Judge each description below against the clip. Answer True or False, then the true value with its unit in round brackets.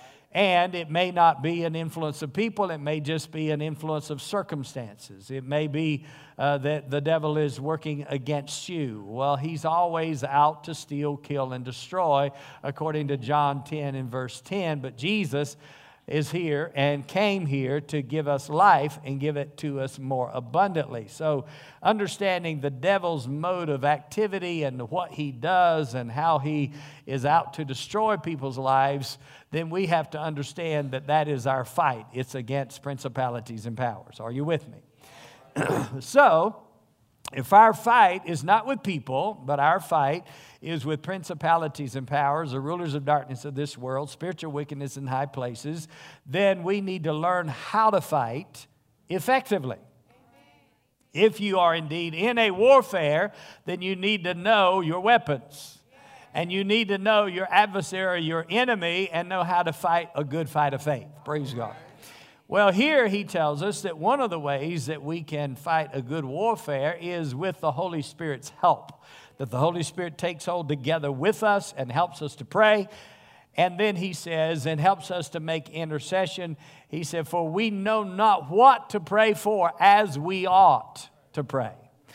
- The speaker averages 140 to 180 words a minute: True (170 wpm)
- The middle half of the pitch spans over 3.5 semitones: True (4.2 semitones)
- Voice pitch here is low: False (155 Hz)